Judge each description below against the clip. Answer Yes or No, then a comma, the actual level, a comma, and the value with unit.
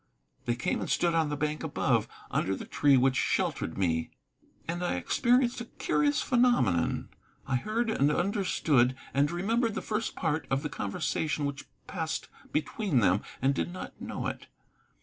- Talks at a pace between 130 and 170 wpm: Yes, average, 165 wpm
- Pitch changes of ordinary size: No, wide, 6.8 semitones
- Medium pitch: Yes, medium, 150 Hz